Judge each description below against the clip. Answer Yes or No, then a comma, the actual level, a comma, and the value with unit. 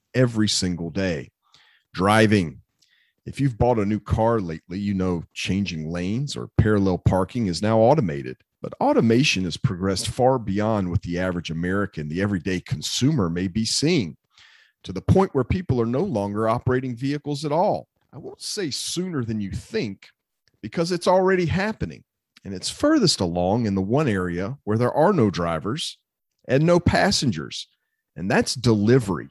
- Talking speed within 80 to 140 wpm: No, average, 160 wpm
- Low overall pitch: Yes, low, 110 Hz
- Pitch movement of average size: No, wide, 5.8 semitones